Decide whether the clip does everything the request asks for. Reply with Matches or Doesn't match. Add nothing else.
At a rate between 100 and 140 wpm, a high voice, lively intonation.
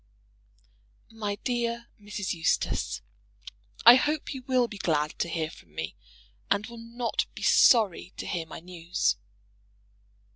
Matches